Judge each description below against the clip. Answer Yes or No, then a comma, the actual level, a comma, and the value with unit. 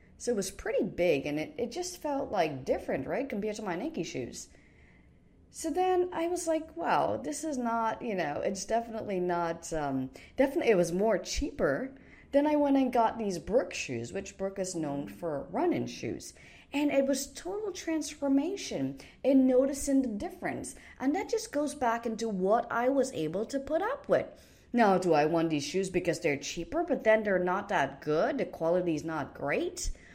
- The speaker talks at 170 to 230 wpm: Yes, average, 190 wpm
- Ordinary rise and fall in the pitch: No, wide, 9.0 semitones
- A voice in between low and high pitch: No, high, 220 Hz